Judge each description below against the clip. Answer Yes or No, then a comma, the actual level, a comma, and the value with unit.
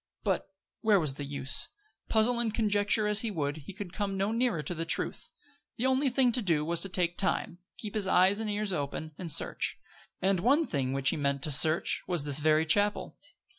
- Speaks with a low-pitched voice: No, medium, 185 Hz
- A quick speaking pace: Yes, fast, 210 wpm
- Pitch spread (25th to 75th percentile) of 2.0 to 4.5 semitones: No, wide, 5.6 semitones